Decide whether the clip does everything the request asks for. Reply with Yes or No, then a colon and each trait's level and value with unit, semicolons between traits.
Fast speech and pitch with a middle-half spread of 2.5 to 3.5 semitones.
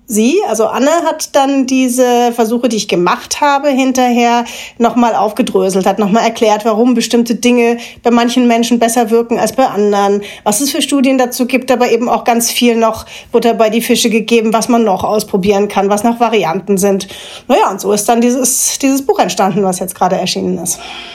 Yes: fast, 195 wpm; average, 3.0 semitones